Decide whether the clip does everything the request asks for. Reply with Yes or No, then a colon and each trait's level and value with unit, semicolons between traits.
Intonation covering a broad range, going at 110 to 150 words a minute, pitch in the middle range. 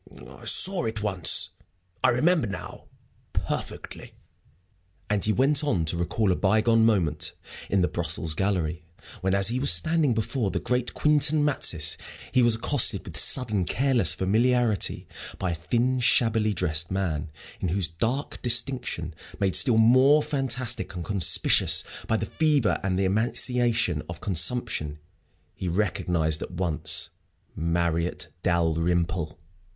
No: wide, 6.1 semitones; slow, 135 wpm; low, 105 Hz